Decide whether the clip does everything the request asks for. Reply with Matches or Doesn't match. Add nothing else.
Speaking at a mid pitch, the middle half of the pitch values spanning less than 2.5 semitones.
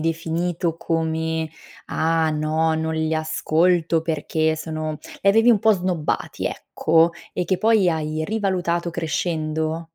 Matches